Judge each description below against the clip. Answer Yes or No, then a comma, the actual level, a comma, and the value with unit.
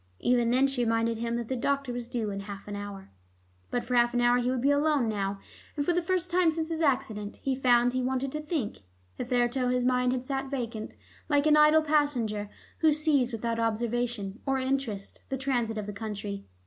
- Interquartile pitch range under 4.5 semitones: Yes, average, 3.4 semitones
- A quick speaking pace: Yes, fast, 215 wpm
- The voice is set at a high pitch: Yes, high, 245 Hz